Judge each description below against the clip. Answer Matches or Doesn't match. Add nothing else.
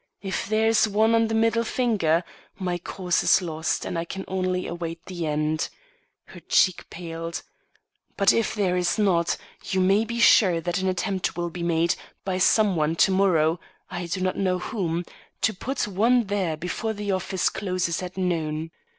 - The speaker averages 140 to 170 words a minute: Doesn't match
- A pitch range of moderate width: Matches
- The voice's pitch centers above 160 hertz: Matches